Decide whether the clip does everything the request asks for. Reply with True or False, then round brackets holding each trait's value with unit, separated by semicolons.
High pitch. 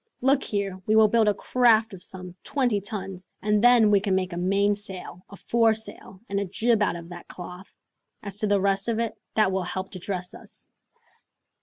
True (200 Hz)